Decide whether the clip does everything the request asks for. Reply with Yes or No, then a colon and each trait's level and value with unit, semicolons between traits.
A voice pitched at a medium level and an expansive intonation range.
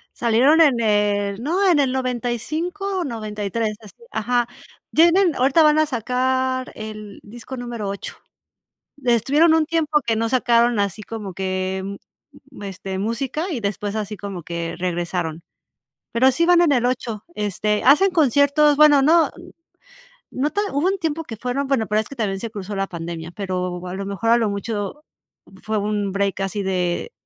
No: high, 230 Hz; wide, 5.9 semitones